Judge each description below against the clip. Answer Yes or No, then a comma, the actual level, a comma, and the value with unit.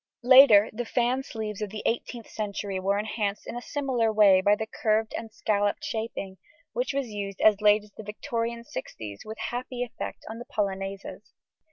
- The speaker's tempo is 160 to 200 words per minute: Yes, average, 180 wpm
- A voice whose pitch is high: Yes, high, 215 Hz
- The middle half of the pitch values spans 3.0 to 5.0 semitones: No, narrow, 2.5 semitones